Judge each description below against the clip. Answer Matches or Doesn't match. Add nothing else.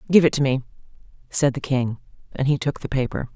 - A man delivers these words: Doesn't match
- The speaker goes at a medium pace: Doesn't match